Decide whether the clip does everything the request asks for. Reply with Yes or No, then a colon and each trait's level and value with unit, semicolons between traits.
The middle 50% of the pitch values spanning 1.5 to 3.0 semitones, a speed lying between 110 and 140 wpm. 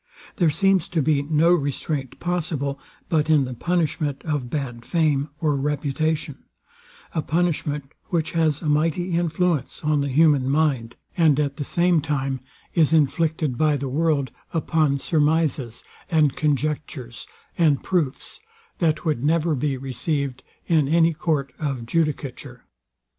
Yes: average, 2.7 semitones; slow, 135 wpm